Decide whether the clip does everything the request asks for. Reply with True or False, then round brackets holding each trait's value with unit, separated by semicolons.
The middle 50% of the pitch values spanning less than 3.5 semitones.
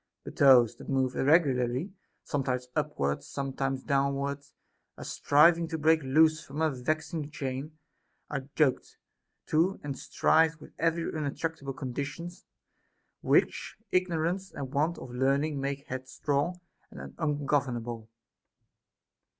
True (3.1 semitones)